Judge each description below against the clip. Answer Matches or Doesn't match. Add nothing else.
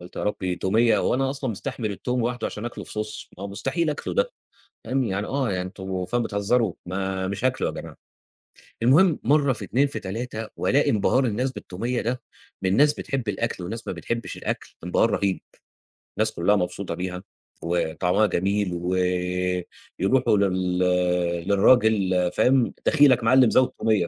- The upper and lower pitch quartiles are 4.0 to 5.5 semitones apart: Matches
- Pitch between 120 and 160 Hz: Doesn't match